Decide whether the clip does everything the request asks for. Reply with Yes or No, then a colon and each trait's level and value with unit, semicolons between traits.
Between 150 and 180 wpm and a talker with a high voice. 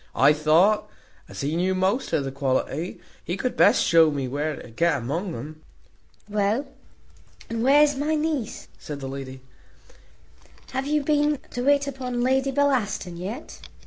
Yes: average, 155 wpm; high, 200 Hz